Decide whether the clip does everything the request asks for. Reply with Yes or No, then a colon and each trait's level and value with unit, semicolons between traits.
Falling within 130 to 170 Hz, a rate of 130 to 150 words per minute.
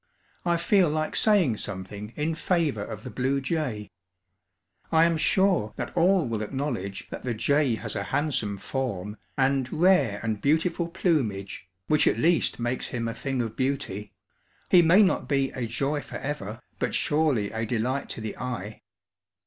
No: low, 135 Hz; average, 165 wpm